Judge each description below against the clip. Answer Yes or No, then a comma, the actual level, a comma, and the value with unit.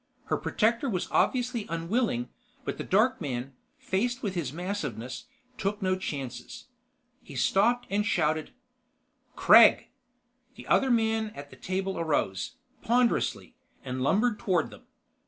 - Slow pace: Yes, slow, 130 wpm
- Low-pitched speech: No, high, 190 Hz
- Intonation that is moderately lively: No, wide, 7.4 semitones